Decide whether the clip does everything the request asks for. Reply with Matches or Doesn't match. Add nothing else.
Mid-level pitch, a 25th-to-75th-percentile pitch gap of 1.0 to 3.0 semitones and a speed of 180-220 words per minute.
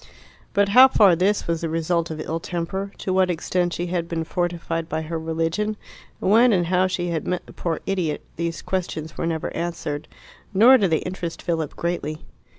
Matches